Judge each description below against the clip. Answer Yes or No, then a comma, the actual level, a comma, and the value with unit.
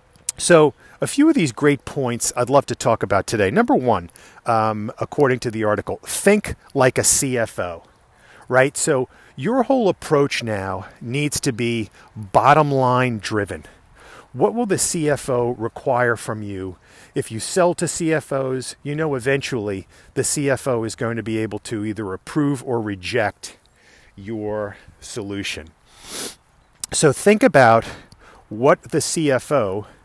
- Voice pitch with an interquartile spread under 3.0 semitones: No, average, 4.7 semitones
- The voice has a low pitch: Yes, low, 125 Hz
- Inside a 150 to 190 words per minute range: No, average, 140 wpm